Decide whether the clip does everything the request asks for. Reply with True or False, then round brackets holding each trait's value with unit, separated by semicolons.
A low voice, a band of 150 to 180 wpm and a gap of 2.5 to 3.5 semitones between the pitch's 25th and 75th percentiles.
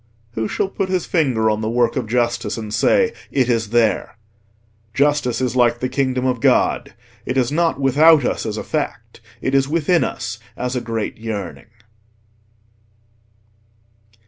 False (125 Hz; 155 wpm; 4.0 semitones)